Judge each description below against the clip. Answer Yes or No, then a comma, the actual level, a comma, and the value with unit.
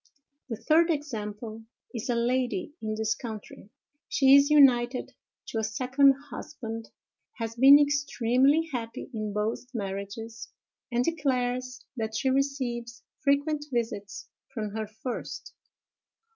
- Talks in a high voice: Yes, high, 245 Hz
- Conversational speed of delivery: No, slow, 120 wpm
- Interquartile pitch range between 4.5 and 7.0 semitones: No, average, 3.8 semitones